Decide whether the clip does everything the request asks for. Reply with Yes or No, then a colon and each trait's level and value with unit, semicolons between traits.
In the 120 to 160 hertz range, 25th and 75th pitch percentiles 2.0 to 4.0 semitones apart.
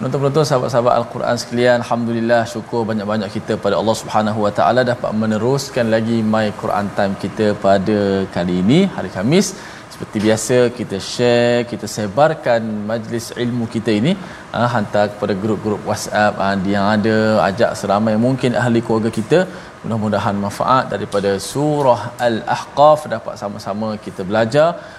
No: low, 110 Hz; narrow, 2.6 semitones